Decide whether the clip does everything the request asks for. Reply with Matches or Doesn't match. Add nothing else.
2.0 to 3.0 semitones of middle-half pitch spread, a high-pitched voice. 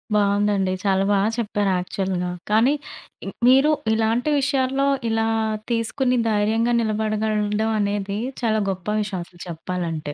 Matches